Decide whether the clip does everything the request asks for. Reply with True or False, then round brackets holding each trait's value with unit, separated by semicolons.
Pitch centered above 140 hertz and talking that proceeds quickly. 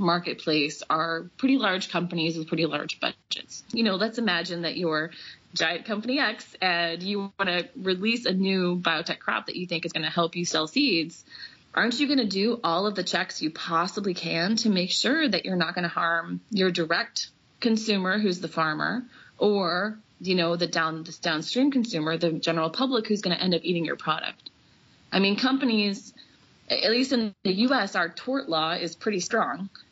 False (185 Hz; 195 wpm)